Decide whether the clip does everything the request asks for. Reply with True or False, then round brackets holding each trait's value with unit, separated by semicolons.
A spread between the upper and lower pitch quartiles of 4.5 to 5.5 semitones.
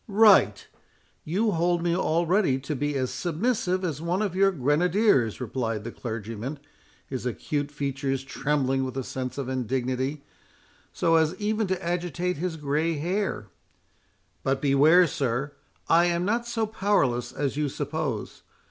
True (5.2 semitones)